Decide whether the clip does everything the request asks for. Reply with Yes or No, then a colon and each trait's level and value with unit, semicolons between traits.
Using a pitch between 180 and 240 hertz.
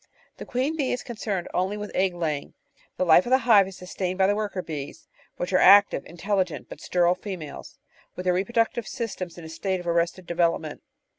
Yes: medium, 185 Hz